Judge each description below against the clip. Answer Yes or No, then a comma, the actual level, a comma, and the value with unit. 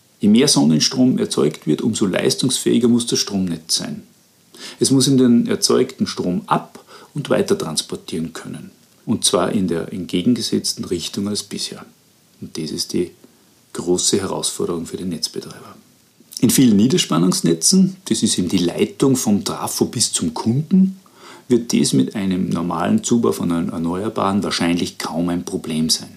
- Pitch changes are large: Yes, wide, 6.7 semitones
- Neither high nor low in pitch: No, low, 100 Hz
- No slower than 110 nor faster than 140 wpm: No, average, 150 wpm